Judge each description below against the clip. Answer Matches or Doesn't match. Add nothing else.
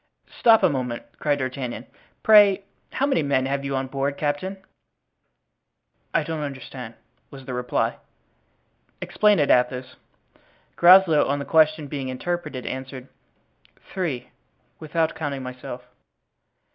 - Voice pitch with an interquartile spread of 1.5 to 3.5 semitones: Doesn't match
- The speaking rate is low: Matches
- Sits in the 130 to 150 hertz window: Matches